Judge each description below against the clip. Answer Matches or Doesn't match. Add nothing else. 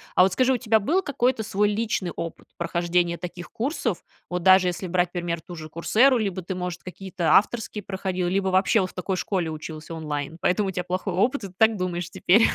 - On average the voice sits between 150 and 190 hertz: Matches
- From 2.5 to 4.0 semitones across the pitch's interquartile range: Matches